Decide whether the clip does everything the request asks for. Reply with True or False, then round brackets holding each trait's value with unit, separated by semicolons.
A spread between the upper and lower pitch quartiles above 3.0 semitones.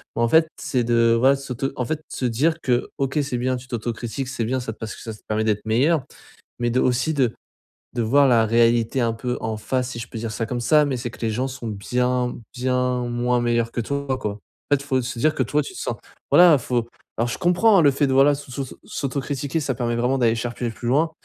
False (2.7 semitones)